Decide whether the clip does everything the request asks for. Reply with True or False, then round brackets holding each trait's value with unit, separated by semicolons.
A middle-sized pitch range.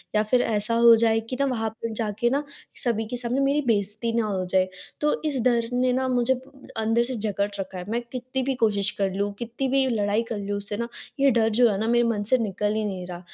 True (3.1 semitones)